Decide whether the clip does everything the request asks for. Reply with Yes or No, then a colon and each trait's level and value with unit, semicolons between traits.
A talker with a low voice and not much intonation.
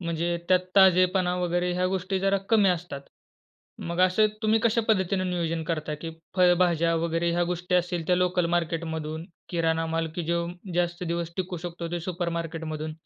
No: medium, 175 Hz; narrow, 1.5 semitones